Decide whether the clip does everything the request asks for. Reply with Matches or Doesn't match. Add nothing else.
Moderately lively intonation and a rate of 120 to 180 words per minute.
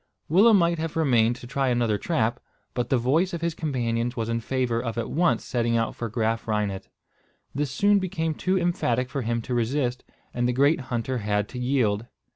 Doesn't match